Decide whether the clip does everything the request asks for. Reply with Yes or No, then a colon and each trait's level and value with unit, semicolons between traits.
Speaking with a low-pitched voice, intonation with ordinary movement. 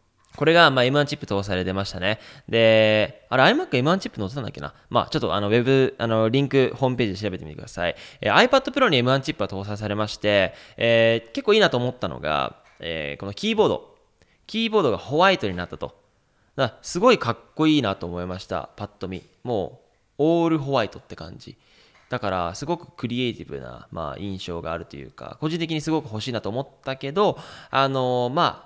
No: low, 120 Hz; wide, 7.4 semitones